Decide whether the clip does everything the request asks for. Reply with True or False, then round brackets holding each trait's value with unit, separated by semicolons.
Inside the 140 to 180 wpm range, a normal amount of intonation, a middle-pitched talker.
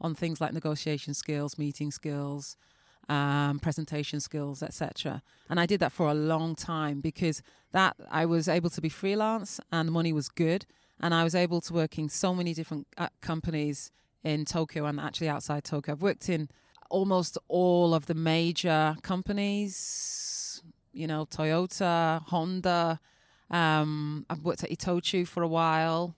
False (160 wpm; 2.3 semitones; 160 Hz)